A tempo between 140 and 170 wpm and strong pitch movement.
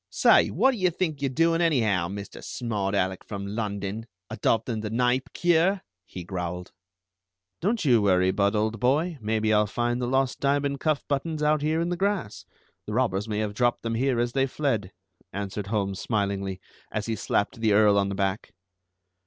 No: average, 185 wpm; wide, 5.8 semitones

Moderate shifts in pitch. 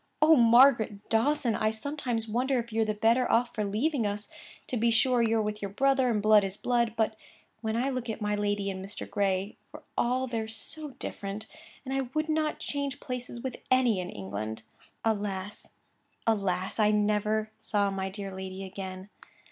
Yes: average, 3.4 semitones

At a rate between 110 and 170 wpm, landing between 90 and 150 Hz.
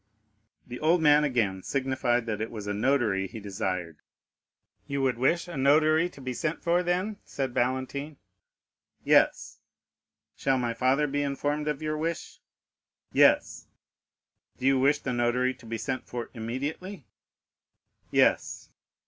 Yes: average, 140 wpm; low, 135 Hz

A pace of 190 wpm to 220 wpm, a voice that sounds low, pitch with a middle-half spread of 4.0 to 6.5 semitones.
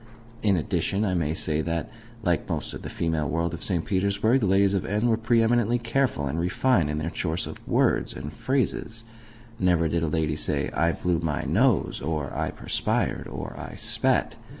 Yes: average, 195 wpm; very low, 90 Hz; wide, 5.4 semitones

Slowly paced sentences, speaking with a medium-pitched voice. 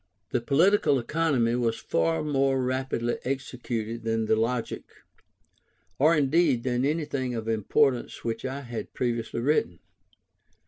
No: slow, 125 wpm; low, 125 Hz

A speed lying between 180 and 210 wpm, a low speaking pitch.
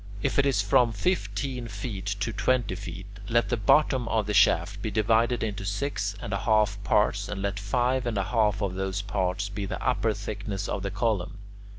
Yes: average, 200 wpm; low, 105 Hz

